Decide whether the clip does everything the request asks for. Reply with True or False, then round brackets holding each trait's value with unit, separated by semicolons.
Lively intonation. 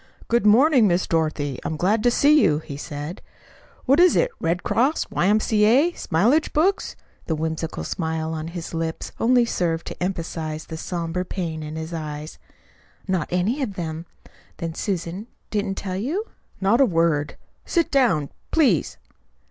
True (6.5 semitones)